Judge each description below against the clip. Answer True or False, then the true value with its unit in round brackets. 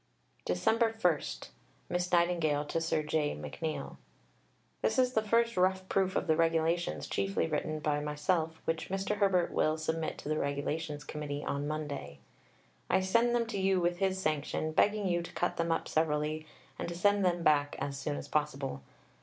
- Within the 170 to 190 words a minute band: True (175 wpm)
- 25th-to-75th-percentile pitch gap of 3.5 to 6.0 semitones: True (3.9 semitones)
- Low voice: False (160 Hz)